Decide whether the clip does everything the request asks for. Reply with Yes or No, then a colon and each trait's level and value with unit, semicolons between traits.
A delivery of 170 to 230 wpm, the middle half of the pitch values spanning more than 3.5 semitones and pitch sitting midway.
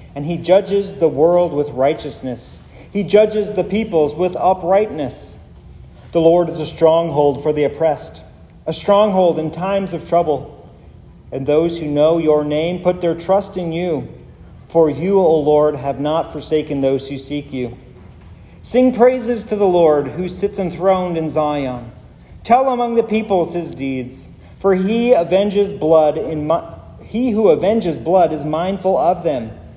No: average, 160 wpm; average, 4.7 semitones; medium, 165 Hz